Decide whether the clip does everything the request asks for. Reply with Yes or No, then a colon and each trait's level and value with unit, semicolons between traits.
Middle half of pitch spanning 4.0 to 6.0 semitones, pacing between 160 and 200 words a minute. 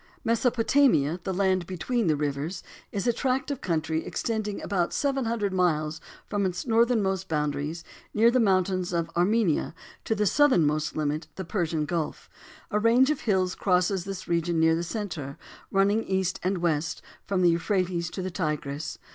Yes: average, 4.5 semitones; average, 165 wpm